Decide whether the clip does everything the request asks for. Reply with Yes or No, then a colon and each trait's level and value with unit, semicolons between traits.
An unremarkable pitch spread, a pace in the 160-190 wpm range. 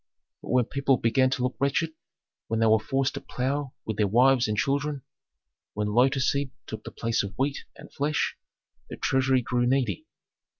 Yes: average, 3.3 semitones; average, 180 wpm